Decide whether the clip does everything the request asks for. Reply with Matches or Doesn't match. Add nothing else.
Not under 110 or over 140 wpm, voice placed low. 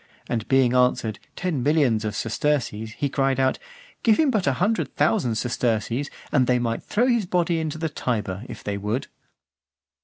Doesn't match